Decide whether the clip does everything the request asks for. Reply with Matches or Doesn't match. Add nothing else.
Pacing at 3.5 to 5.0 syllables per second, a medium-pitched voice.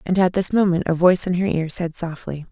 Doesn't match